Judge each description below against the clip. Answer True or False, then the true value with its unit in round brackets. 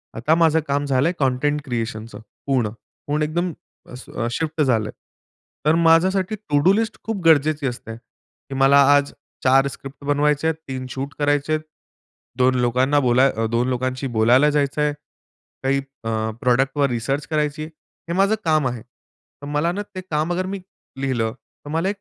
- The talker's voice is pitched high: False (140 Hz)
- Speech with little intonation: False (3.3 semitones)